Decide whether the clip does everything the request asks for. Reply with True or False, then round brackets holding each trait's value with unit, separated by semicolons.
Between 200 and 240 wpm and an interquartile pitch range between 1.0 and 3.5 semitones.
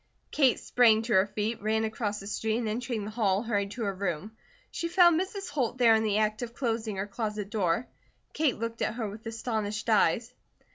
True (205 wpm; 2.4 semitones)